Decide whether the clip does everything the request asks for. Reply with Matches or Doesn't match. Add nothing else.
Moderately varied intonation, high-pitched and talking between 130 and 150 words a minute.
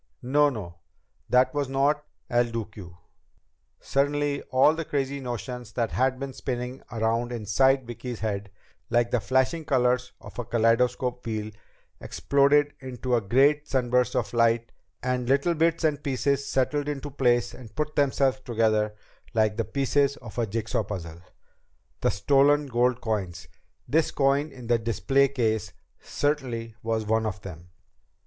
Doesn't match